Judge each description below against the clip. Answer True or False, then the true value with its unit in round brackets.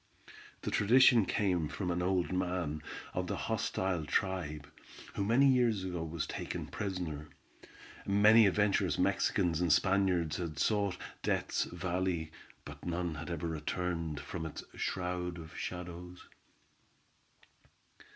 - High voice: False (90 Hz)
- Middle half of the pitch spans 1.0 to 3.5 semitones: True (2.7 semitones)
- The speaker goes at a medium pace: False (120 wpm)